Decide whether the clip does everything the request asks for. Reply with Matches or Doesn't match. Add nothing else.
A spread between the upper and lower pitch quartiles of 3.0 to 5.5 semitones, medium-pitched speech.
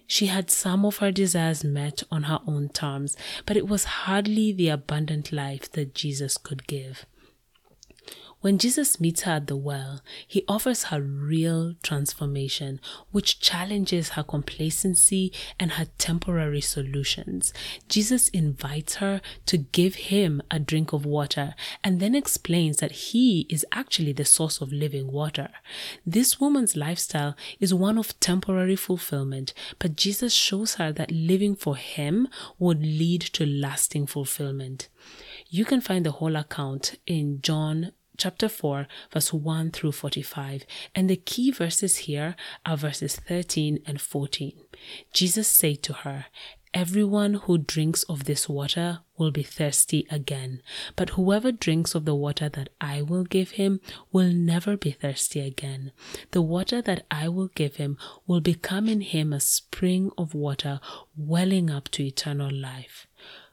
Matches